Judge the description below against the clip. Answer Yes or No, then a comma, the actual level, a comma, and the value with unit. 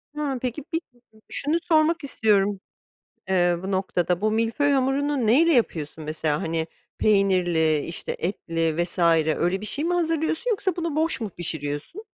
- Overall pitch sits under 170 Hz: No, high, 215 Hz